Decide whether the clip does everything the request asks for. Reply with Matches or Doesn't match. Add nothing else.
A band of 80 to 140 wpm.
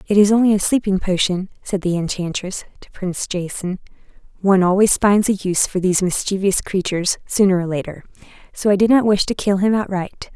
Doesn't match